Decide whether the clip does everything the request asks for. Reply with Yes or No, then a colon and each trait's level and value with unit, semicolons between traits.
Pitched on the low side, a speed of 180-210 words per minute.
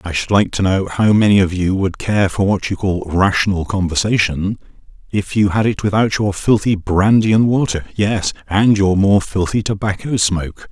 Yes: low, 100 Hz; average, 190 wpm